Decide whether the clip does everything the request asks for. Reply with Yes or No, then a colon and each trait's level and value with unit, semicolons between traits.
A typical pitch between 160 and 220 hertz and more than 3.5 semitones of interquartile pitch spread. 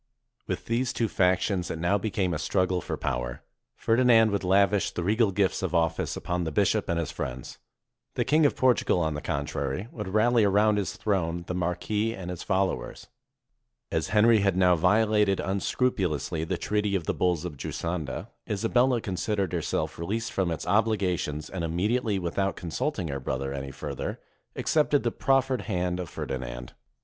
No: very low, 95 Hz; average, 4.3 semitones